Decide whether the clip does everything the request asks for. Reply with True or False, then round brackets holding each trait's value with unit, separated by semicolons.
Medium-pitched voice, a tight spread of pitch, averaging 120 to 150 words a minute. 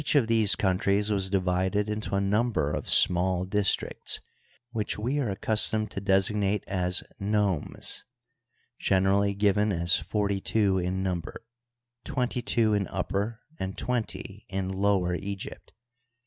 False (100 Hz; 2.0 semitones; 135 wpm)